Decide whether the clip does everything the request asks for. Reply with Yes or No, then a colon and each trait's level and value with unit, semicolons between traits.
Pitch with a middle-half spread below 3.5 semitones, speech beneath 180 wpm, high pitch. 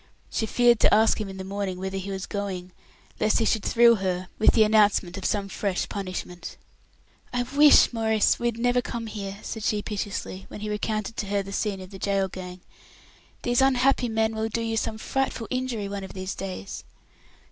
No: average, 2.9 semitones; average, 200 wpm; high, 210 Hz